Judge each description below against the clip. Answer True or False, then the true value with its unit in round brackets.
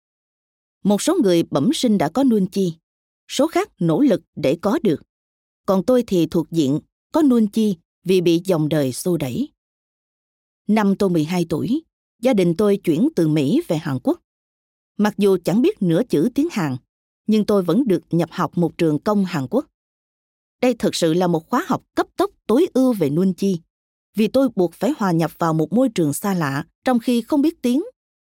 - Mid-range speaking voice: False (195 Hz)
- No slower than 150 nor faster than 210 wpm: True (195 wpm)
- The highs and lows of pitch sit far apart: True (7.1 semitones)